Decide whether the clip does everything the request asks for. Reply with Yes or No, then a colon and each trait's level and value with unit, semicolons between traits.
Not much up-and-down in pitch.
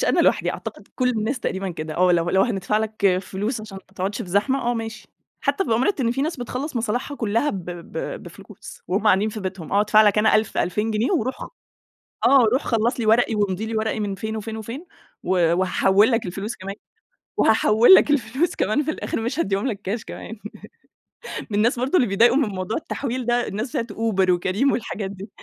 No: average, 3.7 semitones